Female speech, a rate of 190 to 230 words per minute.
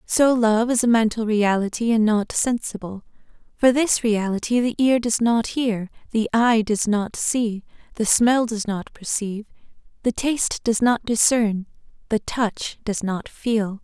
No: female; average, 160 wpm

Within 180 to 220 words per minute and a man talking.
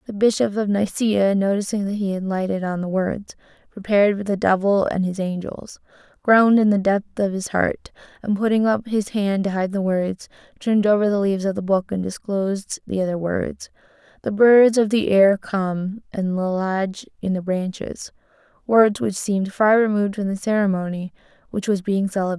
No: average, 190 wpm; female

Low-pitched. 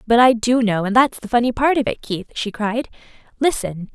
No: high, 230 Hz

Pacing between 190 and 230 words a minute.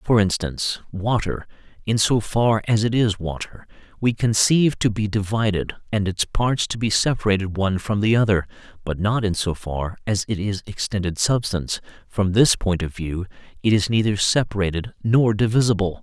No: average, 170 wpm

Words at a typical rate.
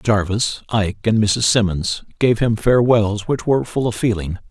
Yes: average, 175 wpm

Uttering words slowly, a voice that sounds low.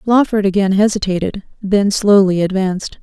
No: slow, 120 wpm; high, 200 Hz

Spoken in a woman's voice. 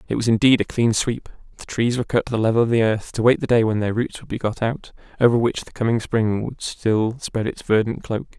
No: male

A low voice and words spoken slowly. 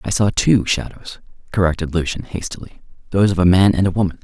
No: very low, 95 Hz; average, 200 wpm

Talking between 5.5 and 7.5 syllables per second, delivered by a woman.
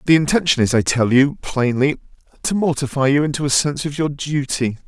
No: 5.7 syllables/s; male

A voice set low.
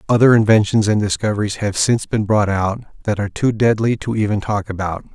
Yes: low, 105 Hz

